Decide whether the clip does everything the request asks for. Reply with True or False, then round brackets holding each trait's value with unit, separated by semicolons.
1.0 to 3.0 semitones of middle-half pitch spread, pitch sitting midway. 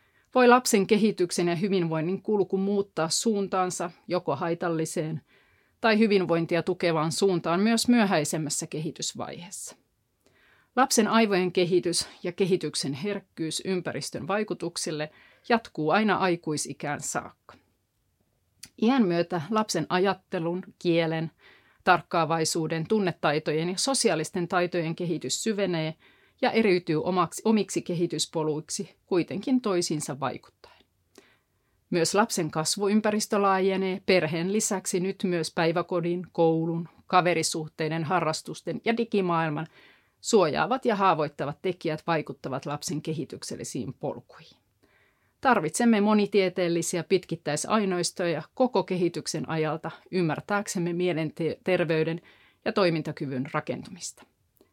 False (3.6 semitones; 175 Hz)